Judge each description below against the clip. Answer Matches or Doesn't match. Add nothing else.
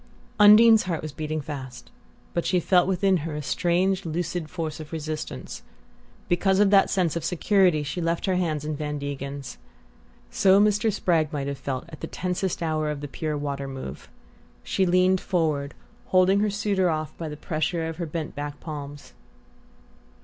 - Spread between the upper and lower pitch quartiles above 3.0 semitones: Matches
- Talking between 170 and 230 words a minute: Matches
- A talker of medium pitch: Matches